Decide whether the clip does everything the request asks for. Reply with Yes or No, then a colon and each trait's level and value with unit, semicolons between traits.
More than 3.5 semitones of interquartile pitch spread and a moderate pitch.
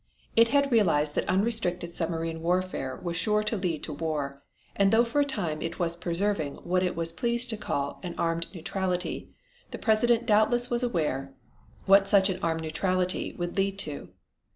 Yes: average, 4.3 semitones; medium, 180 Hz